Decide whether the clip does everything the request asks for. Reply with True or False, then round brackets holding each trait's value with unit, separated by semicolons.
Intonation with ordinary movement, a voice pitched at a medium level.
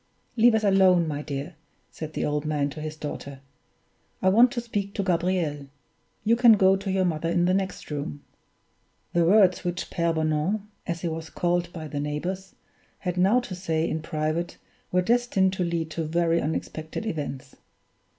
True (3.6 semitones; 170 Hz)